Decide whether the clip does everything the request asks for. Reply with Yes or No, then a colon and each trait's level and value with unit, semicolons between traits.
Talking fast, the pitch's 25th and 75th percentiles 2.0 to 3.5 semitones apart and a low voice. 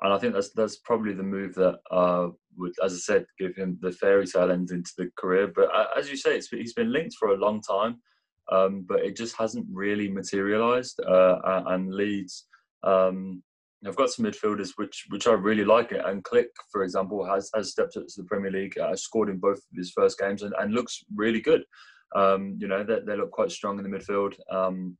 Yes: fast, 225 wpm; narrow, 2.4 semitones; low, 100 Hz